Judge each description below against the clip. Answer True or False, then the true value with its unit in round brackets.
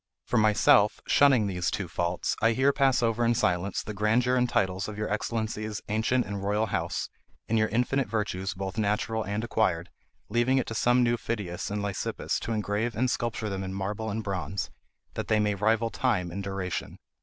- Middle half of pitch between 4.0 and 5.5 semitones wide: False (2.8 semitones)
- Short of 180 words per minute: False (190 wpm)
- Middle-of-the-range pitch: False (105 Hz)